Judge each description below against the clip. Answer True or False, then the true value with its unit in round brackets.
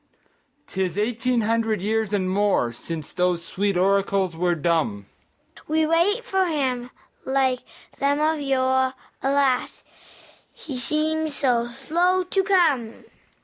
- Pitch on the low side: False (250 Hz)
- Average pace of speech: False (120 wpm)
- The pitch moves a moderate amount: False (7.3 semitones)